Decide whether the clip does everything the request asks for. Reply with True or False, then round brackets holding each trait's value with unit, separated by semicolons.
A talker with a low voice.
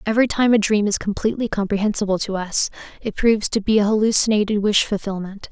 False (210 Hz)